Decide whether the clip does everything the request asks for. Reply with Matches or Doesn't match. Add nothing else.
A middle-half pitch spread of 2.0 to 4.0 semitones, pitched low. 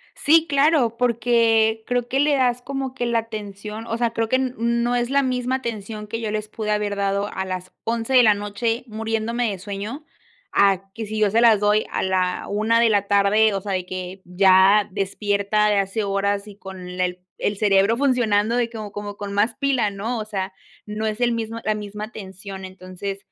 Doesn't match